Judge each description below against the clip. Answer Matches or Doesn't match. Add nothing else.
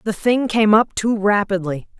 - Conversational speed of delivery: Matches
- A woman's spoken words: Matches